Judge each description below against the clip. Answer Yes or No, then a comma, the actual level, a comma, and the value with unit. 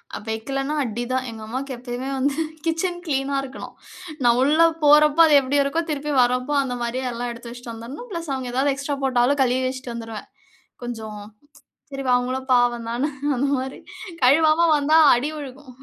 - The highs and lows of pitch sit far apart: No, average, 2.9 semitones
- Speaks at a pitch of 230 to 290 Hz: Yes, very high, 260 Hz